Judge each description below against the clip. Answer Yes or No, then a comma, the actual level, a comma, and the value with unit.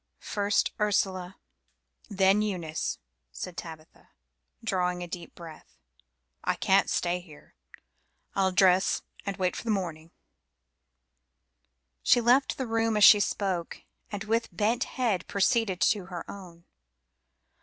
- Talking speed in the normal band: No, slow, 125 wpm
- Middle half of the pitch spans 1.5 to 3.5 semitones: Yes, average, 2.9 semitones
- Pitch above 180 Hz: Yes, high, 190 Hz